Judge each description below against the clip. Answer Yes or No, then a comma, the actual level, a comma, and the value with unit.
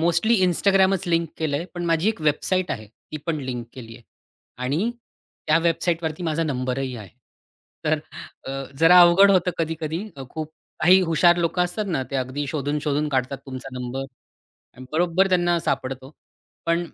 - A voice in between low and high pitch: Yes, medium, 160 Hz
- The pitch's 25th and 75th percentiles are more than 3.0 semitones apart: Yes, average, 4.4 semitones